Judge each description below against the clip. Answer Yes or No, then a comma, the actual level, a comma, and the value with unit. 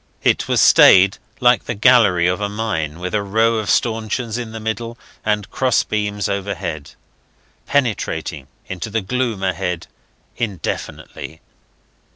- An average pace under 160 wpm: Yes, slow, 135 wpm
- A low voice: Yes, low, 105 Hz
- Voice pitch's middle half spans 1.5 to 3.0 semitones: No, average, 3.4 semitones